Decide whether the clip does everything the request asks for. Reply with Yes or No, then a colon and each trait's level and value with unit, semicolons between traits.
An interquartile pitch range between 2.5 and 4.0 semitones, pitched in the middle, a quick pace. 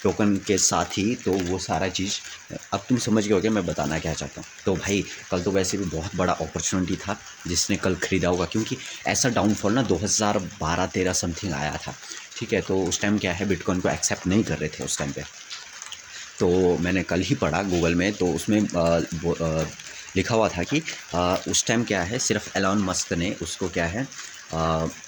No: average, 2.9 semitones; very low, 95 Hz; fast, 205 wpm